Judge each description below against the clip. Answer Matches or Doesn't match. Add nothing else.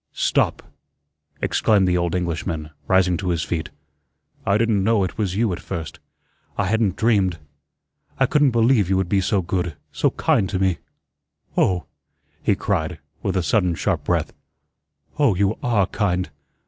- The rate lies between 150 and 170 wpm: Matches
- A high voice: Doesn't match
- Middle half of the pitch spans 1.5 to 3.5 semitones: Matches